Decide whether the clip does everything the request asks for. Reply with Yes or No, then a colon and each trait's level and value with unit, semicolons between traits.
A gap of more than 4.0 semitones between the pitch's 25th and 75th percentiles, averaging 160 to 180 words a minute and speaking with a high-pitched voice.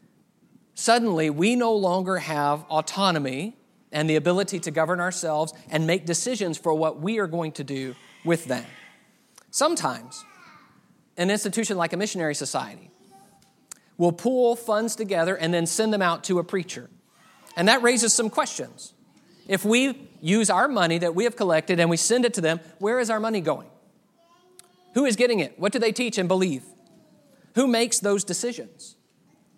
Yes: wide, 5.4 semitones; average, 165 wpm; high, 195 Hz